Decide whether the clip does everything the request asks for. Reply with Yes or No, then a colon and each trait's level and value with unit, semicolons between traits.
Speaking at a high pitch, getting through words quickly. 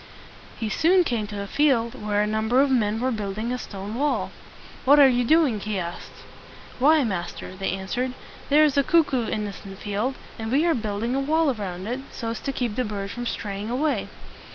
Yes: high, 230 Hz; fast, 210 wpm